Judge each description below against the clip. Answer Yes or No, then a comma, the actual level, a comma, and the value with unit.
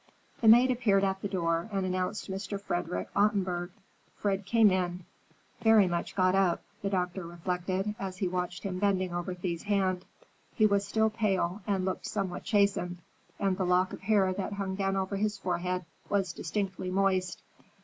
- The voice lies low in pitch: No, high, 190 Hz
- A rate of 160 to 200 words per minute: Yes, average, 170 wpm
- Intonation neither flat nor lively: No, narrow, 1.9 semitones